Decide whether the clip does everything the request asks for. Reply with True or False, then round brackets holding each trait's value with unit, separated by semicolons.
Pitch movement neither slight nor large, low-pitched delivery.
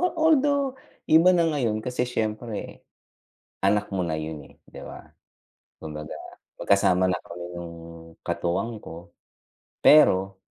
False (8.6 semitones; 100 Hz)